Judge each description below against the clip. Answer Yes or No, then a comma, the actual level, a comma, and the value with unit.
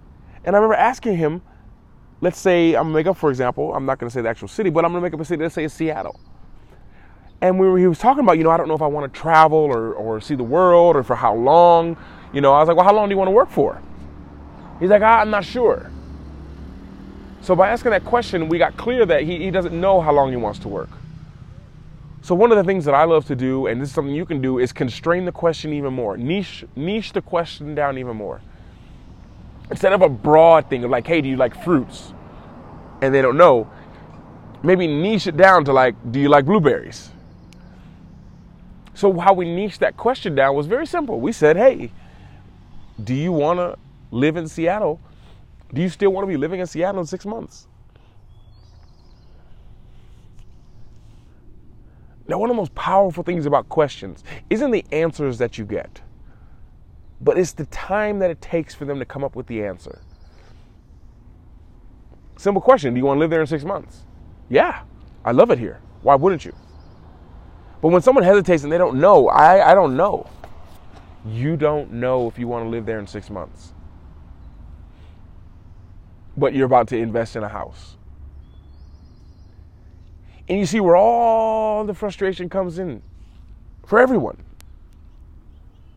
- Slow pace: No, average, 190 wpm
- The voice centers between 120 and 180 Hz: Yes, medium, 140 Hz